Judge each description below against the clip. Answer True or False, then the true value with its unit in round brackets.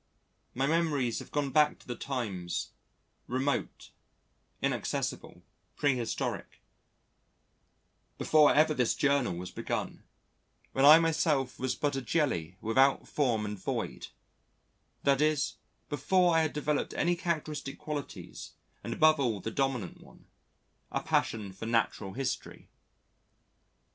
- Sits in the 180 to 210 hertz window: False (135 Hz)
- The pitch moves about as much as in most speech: True (4.2 semitones)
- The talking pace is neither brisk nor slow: False (120 wpm)